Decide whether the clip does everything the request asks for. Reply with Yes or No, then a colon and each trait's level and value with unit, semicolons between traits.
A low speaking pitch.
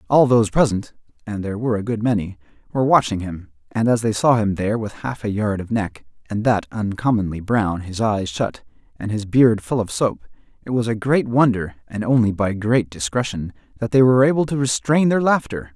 Yes: low, 110 Hz